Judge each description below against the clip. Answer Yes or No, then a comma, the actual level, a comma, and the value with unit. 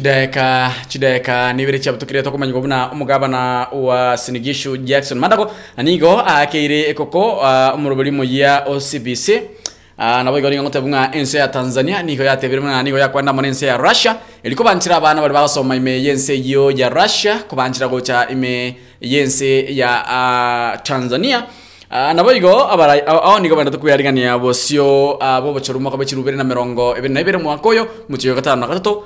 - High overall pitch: No, low, 135 Hz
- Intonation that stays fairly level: Yes, narrow, 2.2 semitones